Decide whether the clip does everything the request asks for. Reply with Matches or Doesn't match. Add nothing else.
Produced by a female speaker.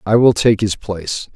Doesn't match